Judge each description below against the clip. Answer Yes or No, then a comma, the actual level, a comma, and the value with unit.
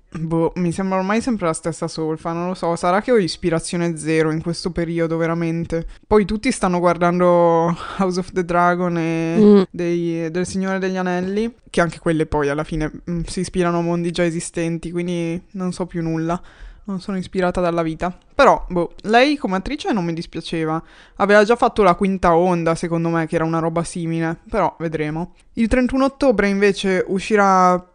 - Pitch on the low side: No, medium, 175 Hz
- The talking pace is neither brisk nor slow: No, fast, 180 wpm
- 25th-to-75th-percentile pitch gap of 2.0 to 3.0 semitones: Yes, narrow, 2.4 semitones